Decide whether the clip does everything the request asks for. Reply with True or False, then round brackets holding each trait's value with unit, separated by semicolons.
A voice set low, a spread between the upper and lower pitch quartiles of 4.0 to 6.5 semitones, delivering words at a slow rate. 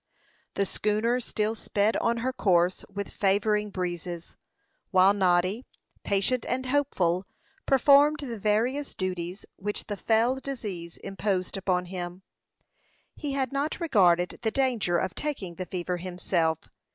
False (200 Hz; 5.2 semitones; 130 wpm)